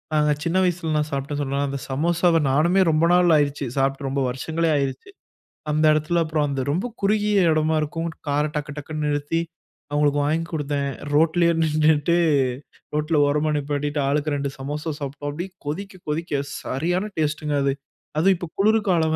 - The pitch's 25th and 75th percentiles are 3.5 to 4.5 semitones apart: No, narrow, 2.5 semitones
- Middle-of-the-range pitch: Yes, medium, 155 Hz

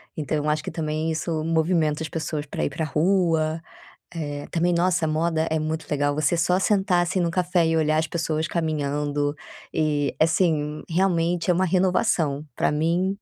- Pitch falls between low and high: Yes, medium, 160 Hz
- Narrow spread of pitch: Yes, narrow, 2.1 semitones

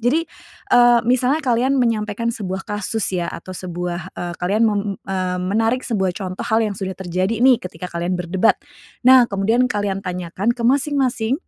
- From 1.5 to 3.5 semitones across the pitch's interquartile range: No, average, 4.6 semitones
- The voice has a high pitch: Yes, high, 210 Hz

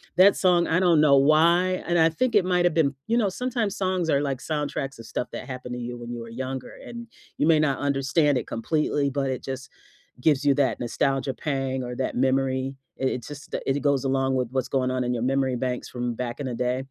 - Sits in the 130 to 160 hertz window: Yes, low, 135 Hz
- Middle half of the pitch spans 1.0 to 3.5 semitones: No, average, 3.9 semitones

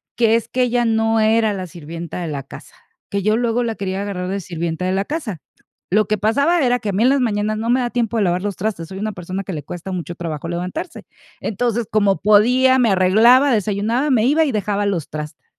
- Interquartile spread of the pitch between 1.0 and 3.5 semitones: No, average, 4.3 semitones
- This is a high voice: Yes, high, 210 Hz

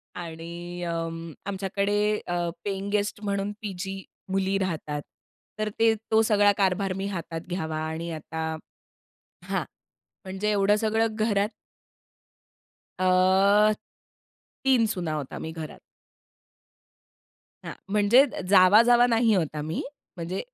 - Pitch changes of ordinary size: Yes, average, 3.6 semitones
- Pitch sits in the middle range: No, high, 195 Hz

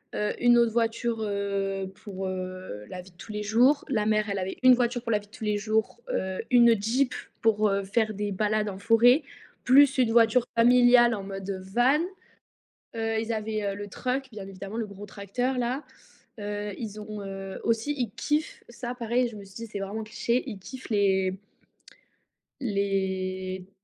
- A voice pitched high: Yes, high, 215 Hz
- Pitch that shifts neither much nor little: Yes, average, 3.2 semitones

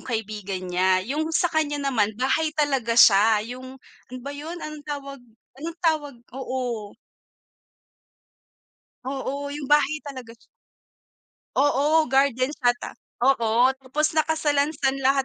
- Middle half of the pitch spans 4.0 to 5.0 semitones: No, average, 3.6 semitones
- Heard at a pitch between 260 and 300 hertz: Yes, very high, 270 Hz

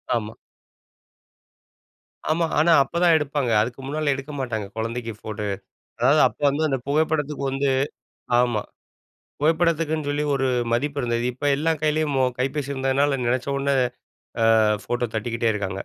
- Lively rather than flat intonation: No, average, 3.8 semitones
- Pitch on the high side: No, low, 135 Hz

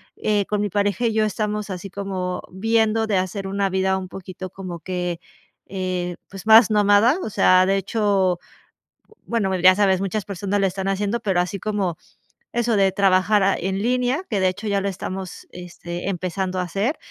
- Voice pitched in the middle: No, high, 195 Hz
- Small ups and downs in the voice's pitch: Yes, narrow, 2.1 semitones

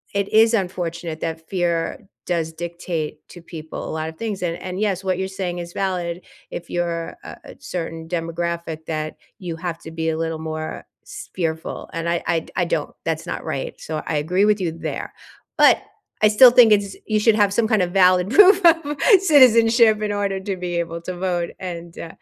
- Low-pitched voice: No, medium, 175 Hz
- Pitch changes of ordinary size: Yes, average, 3.5 semitones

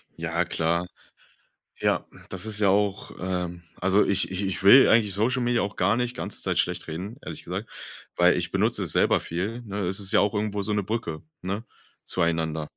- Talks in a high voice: No, low, 100 Hz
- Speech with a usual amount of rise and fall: Yes, average, 3.0 semitones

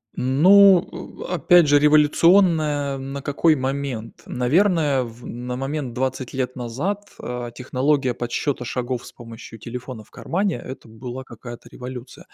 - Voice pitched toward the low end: Yes, low, 130 Hz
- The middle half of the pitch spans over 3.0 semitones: Yes, average, 3.6 semitones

